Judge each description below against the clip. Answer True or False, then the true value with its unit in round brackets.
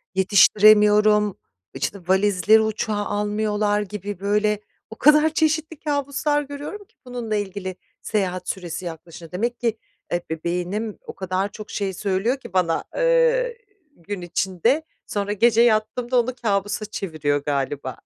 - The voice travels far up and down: False (4.1 semitones)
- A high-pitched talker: True (210 Hz)